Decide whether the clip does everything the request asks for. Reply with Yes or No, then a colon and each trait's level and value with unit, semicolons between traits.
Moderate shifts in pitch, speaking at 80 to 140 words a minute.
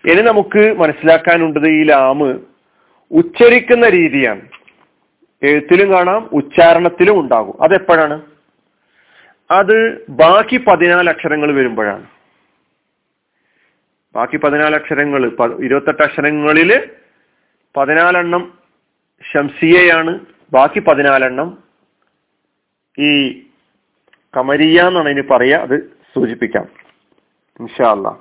No: average, 3.7 semitones; average, 70 wpm